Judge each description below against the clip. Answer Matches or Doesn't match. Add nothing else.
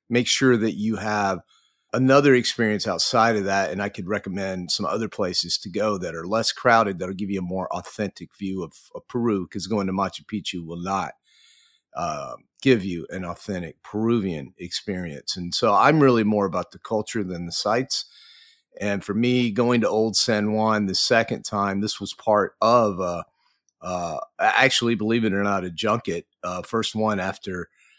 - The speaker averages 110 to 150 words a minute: Doesn't match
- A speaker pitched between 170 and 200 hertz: Doesn't match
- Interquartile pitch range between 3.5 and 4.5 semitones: Doesn't match